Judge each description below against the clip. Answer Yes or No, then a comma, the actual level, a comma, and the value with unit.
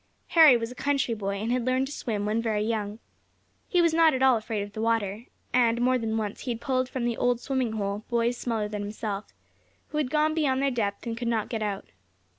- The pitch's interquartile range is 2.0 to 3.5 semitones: Yes, average, 3.2 semitones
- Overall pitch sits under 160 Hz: No, high, 230 Hz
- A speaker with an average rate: No, fast, 235 wpm